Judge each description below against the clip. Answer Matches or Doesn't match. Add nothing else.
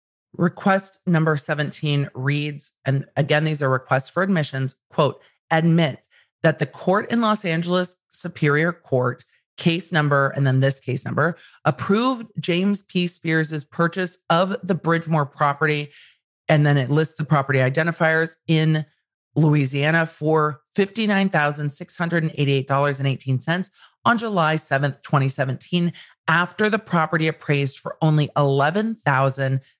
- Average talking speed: Doesn't match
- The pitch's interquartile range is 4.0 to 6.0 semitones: Doesn't match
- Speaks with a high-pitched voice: Doesn't match